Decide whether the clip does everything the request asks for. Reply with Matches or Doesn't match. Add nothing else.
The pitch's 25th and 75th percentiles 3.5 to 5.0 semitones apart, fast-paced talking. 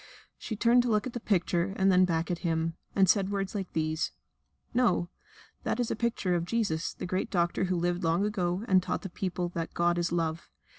Doesn't match